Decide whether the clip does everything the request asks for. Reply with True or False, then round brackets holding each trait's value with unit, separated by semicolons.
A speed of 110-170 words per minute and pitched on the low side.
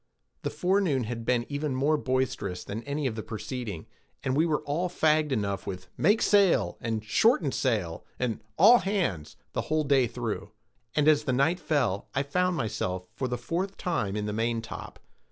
False (180 wpm; 130 Hz)